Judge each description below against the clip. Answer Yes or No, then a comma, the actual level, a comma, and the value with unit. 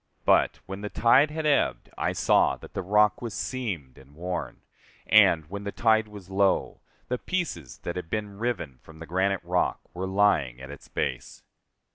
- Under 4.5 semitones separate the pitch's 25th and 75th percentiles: No, average, 4.8 semitones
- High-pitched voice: No, very low, 95 Hz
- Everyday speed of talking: Yes, average, 180 wpm